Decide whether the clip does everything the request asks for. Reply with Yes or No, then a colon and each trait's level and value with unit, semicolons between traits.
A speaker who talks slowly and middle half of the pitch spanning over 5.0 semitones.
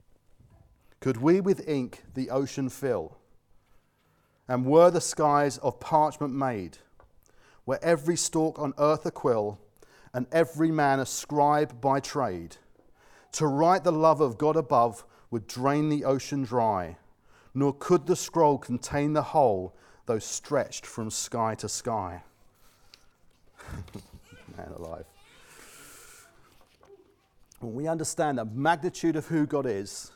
Yes: slow, 125 wpm; wide, 5.6 semitones